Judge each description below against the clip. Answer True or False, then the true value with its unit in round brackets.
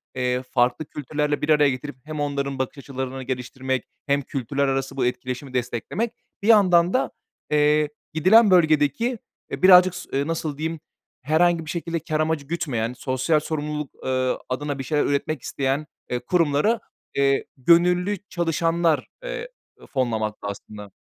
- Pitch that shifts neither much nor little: True (4.0 semitones)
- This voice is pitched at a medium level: True (145 Hz)